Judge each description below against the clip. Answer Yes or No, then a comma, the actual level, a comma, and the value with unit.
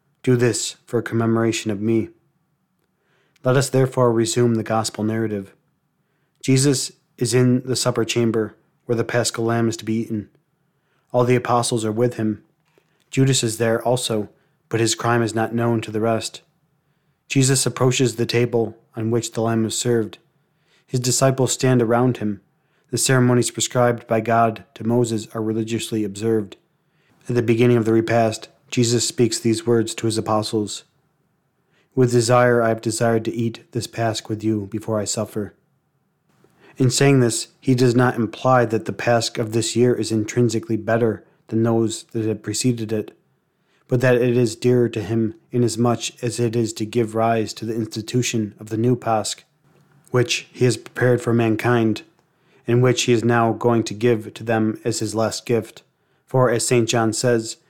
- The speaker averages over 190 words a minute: No, average, 175 wpm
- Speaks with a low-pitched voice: Yes, low, 120 Hz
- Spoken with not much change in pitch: Yes, narrow, 2.1 semitones